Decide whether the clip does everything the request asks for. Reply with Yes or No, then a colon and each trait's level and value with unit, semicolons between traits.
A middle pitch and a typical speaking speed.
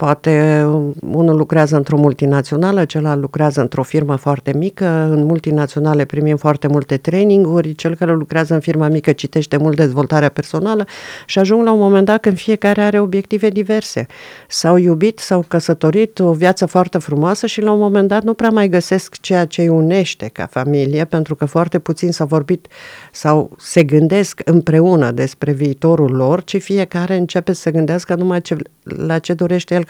No: medium, 165 Hz; fast, 175 wpm